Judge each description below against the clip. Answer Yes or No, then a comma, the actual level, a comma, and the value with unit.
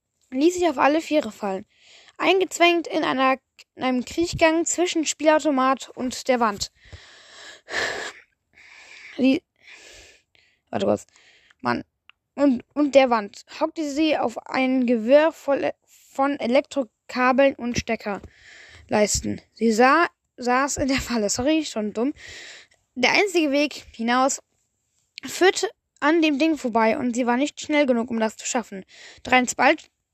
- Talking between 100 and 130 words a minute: Yes, slow, 125 wpm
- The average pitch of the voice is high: Yes, very high, 275 Hz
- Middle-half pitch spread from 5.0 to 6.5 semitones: No, average, 4.3 semitones